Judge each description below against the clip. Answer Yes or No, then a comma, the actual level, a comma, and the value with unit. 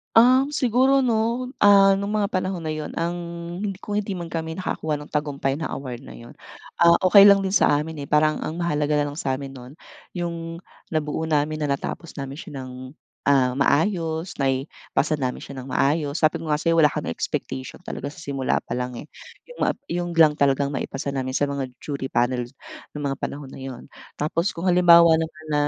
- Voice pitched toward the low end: No, medium, 155 Hz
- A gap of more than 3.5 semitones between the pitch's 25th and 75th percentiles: Yes, average, 4.1 semitones